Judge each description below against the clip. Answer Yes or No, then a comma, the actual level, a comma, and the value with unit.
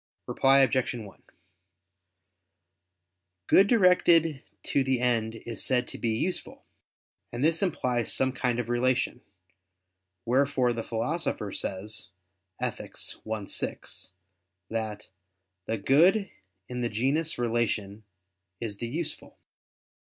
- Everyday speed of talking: No, slow, 110 wpm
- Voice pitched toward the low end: Yes, low, 125 Hz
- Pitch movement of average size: Yes, average, 3.8 semitones